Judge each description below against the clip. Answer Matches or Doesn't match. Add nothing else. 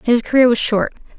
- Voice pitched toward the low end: Doesn't match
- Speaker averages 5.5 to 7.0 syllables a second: Matches